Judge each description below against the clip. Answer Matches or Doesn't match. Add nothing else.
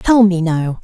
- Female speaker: Matches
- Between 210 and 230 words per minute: Matches